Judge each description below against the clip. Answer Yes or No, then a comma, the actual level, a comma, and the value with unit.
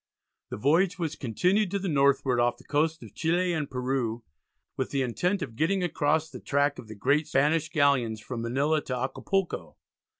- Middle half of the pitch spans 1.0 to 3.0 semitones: No, average, 4.4 semitones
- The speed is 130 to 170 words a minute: No, average, 180 wpm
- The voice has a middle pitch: Yes, medium, 145 Hz